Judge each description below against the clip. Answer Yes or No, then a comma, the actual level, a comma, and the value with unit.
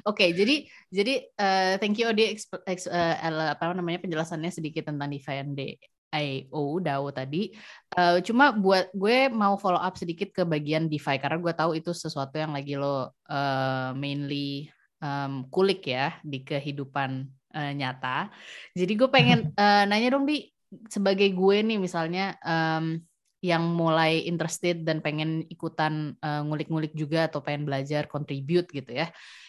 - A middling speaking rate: No, fast, 155 wpm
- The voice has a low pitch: No, medium, 160 Hz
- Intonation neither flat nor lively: Yes, average, 4.6 semitones